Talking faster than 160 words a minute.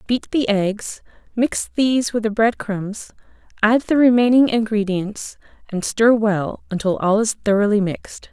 No: average, 150 wpm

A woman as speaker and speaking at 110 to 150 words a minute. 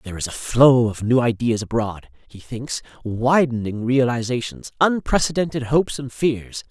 No: male; average, 145 wpm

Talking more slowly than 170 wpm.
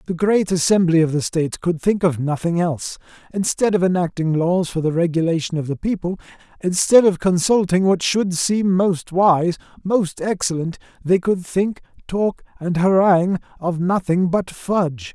Yes: average, 160 wpm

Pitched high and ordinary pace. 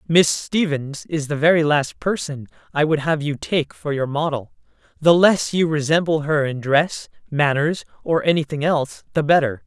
No: medium, 150 Hz; average, 175 wpm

